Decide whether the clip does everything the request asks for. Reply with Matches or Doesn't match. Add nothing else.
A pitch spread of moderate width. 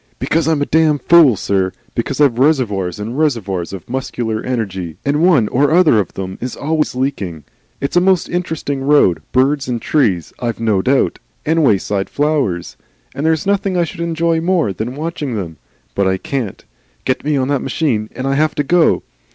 Doesn't match